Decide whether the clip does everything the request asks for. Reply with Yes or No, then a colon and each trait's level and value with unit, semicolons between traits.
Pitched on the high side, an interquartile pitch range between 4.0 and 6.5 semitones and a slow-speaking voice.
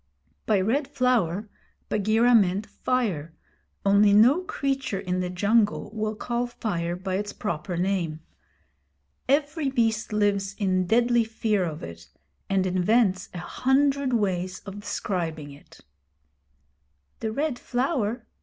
Yes: high, 210 Hz; average, 4.7 semitones; slow, 125 wpm